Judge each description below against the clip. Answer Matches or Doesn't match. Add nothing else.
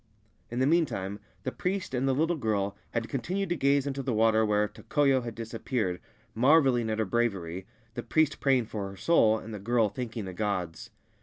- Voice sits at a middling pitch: Doesn't match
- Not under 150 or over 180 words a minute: Doesn't match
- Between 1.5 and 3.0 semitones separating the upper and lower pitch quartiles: Doesn't match